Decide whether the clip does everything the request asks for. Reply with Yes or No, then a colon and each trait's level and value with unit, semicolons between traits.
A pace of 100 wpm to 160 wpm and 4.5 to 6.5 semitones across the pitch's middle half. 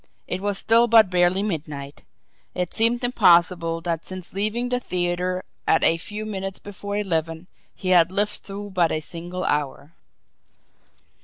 No: average, 150 wpm; average, 3.6 semitones